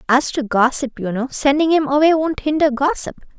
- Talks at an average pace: Yes, average, 195 wpm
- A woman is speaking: Yes, female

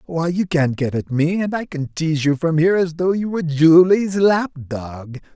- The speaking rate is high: Yes, fast, 215 wpm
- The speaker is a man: Yes, male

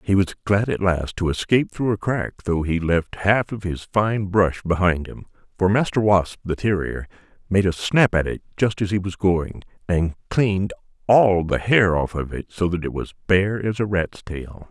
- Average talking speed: No, fast, 210 wpm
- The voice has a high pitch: No, very low, 95 Hz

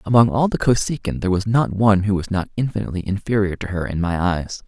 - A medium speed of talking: No, fast, 230 wpm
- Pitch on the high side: No, low, 100 Hz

